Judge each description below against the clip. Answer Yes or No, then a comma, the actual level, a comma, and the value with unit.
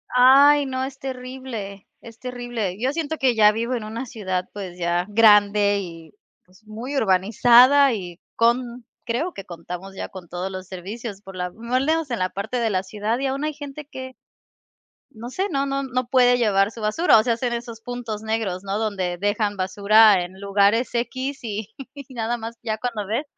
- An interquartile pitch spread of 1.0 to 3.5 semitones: No, average, 4.2 semitones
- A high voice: Yes, high, 225 Hz